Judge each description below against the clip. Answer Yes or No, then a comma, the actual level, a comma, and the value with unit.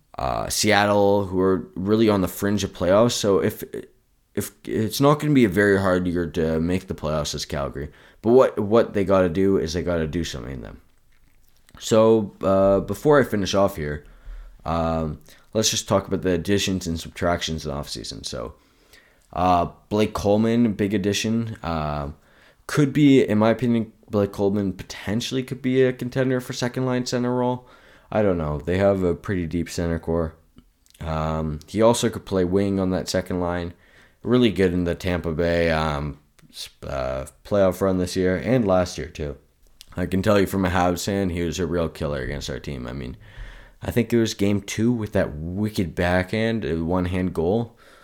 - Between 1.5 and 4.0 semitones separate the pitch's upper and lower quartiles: No, average, 4.4 semitones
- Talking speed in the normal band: Yes, average, 190 wpm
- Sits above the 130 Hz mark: No, very low, 95 Hz